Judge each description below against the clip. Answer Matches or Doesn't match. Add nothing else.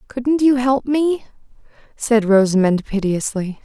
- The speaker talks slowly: Matches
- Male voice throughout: Doesn't match